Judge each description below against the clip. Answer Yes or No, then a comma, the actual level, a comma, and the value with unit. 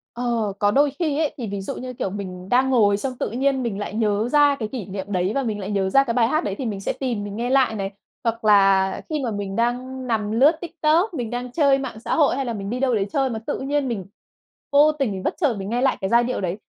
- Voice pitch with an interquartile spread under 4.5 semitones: No, average, 4.8 semitones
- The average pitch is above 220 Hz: Yes, high, 235 Hz